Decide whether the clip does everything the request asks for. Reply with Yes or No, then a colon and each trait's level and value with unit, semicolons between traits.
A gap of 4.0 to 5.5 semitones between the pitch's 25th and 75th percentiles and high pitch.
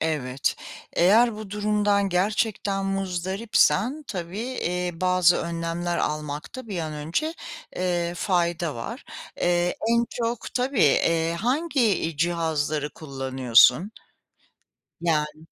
No: average, 4.6 semitones; medium, 175 Hz